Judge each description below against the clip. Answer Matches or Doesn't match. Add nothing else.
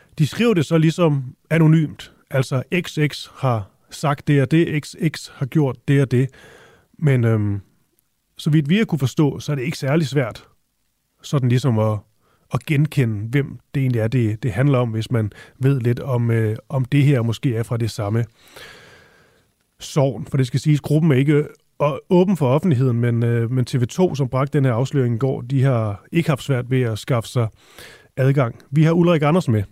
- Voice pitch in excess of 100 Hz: Matches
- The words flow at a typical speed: Matches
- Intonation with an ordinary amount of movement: Matches